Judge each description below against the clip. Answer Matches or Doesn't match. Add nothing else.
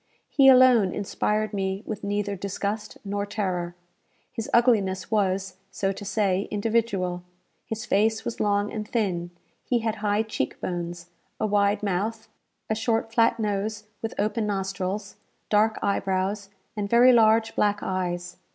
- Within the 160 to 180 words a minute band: Doesn't match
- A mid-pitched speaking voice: Doesn't match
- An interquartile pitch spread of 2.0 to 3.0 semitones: Matches